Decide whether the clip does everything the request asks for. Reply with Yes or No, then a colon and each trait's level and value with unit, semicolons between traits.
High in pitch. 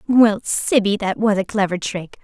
Yes: high, 205 Hz